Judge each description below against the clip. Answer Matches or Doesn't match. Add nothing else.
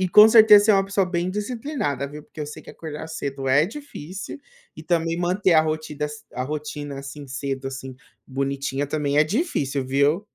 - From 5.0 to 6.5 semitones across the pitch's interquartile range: Matches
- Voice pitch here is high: Doesn't match